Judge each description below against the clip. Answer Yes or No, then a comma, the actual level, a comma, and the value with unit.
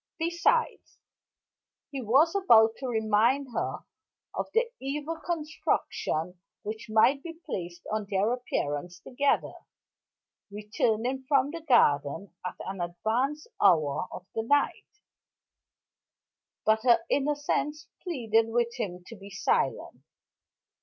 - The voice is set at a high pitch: Yes, high, 230 Hz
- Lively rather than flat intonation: Yes, wide, 6.2 semitones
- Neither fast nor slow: No, slow, 115 wpm